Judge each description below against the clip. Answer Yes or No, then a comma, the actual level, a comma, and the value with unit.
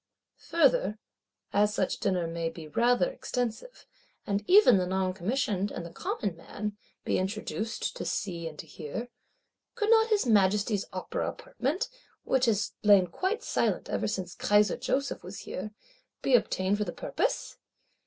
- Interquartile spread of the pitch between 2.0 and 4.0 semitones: No, average, 5.0 semitones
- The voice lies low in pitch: No, high, 210 Hz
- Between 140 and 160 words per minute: Yes, average, 150 wpm